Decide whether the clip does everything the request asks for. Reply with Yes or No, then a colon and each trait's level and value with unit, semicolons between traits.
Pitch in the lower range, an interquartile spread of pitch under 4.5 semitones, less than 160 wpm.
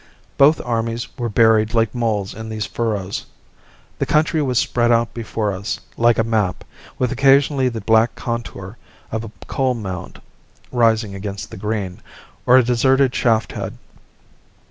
Yes: low, 115 Hz; narrow, 2.4 semitones; average, 150 wpm